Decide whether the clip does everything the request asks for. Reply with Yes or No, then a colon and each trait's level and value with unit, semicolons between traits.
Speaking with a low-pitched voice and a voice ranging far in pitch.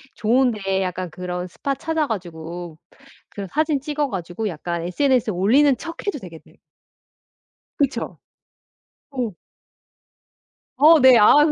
No: high, 220 Hz; wide, 7.9 semitones